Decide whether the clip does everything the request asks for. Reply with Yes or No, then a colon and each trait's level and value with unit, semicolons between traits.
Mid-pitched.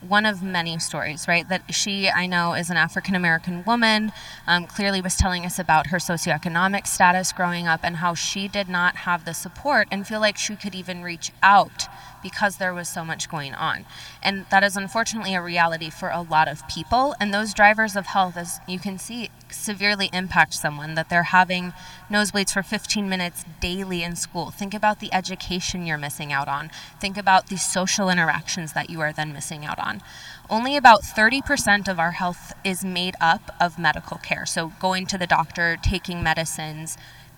Yes: medium, 180 Hz